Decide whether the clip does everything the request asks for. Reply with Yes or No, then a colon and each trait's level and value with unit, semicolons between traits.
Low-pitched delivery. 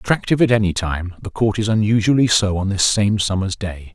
Yes: low, 105 Hz